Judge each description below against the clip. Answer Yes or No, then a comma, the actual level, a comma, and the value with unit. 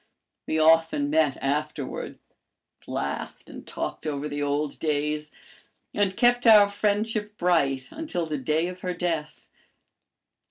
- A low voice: No, medium, 160 Hz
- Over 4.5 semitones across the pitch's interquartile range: Yes, average, 5.3 semitones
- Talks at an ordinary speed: No, slow, 125 wpm